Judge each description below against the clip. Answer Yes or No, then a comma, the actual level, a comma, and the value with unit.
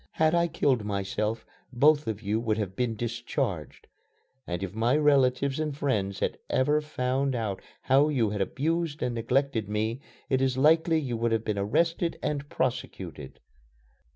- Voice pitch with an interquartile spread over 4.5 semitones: Yes, average, 5.1 semitones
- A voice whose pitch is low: Yes, low, 125 Hz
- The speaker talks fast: No, average, 160 wpm